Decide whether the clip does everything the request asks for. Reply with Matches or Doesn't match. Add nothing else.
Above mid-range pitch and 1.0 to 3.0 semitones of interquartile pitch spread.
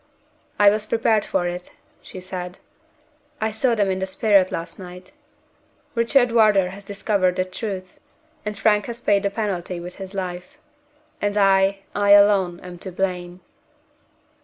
Matches